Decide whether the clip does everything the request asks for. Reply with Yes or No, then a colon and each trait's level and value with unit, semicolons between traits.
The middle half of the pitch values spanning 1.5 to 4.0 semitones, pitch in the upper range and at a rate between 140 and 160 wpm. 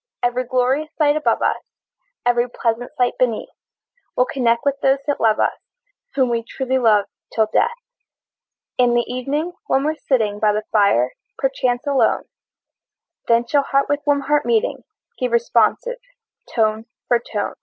Yes: average, 3.1 semitones; high, 245 Hz; average, 155 wpm